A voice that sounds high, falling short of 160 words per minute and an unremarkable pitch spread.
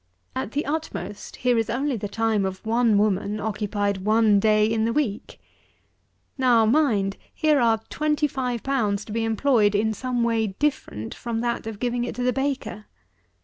No: high, 225 Hz; average, 175 wpm; average, 3.2 semitones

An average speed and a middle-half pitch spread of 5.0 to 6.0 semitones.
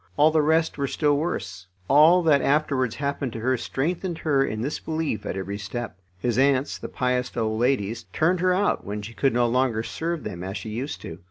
No: fast, 210 wpm; wide, 5.4 semitones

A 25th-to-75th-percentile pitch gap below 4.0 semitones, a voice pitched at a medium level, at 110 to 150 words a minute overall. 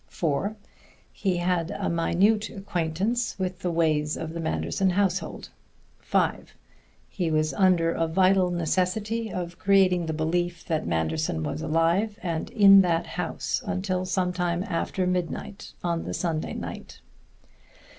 Yes: average, 2.7 semitones; medium, 175 Hz; slow, 135 wpm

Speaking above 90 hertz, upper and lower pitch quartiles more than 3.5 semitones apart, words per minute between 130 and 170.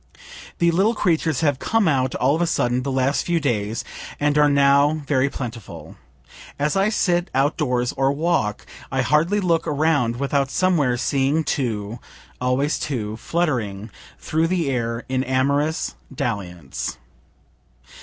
Yes: medium, 140 Hz; average, 4.4 semitones; average, 140 wpm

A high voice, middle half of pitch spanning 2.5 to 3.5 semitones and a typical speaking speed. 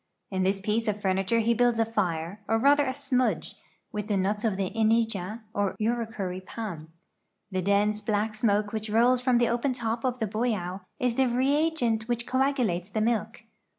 Yes: high, 220 Hz; average, 3.0 semitones; average, 185 wpm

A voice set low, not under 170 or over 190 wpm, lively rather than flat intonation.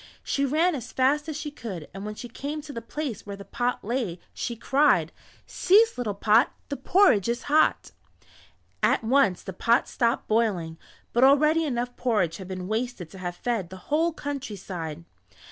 No: high, 240 Hz; average, 180 wpm; wide, 6.5 semitones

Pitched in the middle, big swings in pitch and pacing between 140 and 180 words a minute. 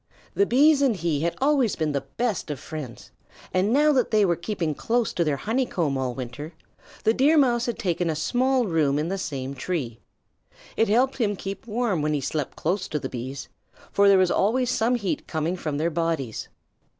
No: medium, 180 Hz; wide, 7.8 semitones; fast, 205 wpm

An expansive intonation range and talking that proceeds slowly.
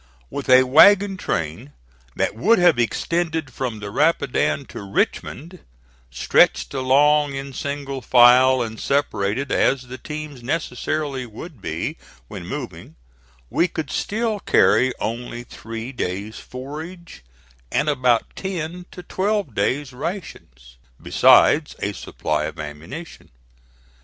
Yes: wide, 5.7 semitones; slow, 120 wpm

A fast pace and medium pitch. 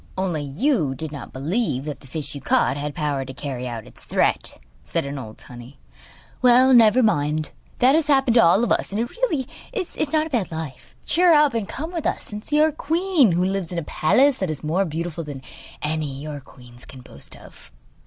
Yes: fast, 220 wpm; medium, 175 Hz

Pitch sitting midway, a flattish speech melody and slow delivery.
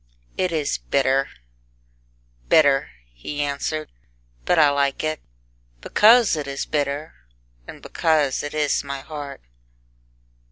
Yes: medium, 145 Hz; narrow, 2.0 semitones; slow, 115 wpm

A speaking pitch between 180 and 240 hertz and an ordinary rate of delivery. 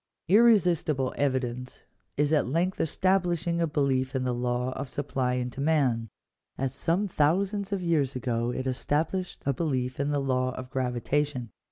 No: medium, 140 Hz; average, 160 wpm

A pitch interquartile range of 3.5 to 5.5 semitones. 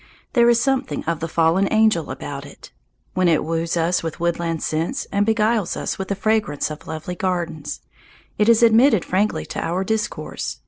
Yes: average, 5.0 semitones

